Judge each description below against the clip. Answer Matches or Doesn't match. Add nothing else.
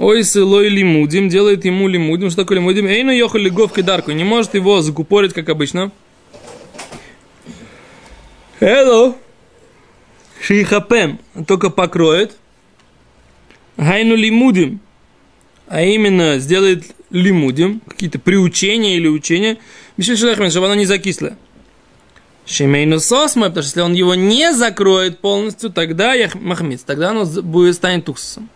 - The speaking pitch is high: Matches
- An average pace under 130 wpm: Matches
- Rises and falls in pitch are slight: Doesn't match